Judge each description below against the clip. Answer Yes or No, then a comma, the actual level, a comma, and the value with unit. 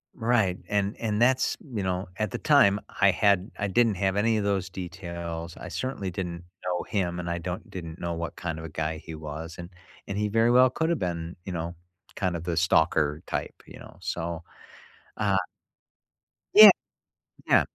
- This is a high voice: No, very low, 90 Hz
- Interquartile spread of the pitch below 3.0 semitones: No, average, 3.3 semitones